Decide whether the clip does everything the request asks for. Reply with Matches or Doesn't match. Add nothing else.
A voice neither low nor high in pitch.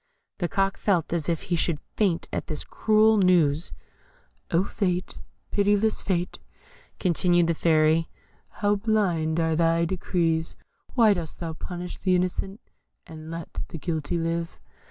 Matches